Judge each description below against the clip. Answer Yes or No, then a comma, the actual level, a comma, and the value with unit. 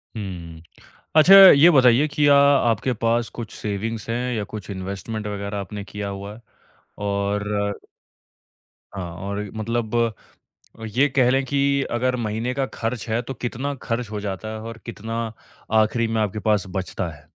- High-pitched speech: No, low, 110 Hz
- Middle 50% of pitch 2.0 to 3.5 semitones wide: Yes, average, 3.2 semitones